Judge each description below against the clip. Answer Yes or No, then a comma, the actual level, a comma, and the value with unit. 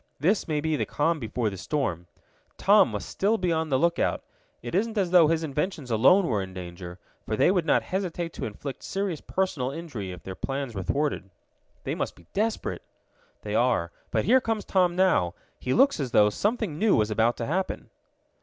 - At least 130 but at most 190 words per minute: No, average, 200 wpm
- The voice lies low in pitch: No, medium, 150 Hz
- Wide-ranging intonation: Yes, wide, 8.8 semitones